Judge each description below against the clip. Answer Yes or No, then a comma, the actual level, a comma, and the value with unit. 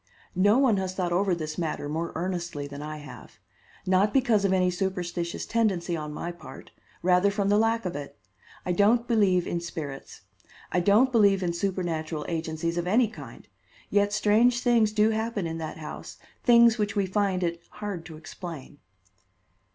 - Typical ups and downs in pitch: Yes, average, 3.8 semitones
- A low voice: No, medium, 185 Hz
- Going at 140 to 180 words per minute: Yes, average, 175 wpm